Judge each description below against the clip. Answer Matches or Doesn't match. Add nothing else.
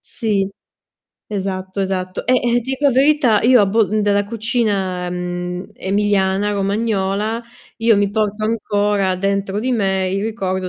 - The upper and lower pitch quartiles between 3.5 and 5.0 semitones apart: Doesn't match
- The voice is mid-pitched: Doesn't match